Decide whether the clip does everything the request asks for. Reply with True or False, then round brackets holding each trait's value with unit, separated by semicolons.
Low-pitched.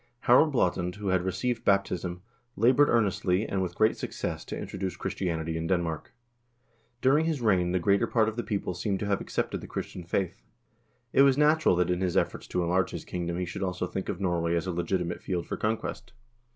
True (95 Hz)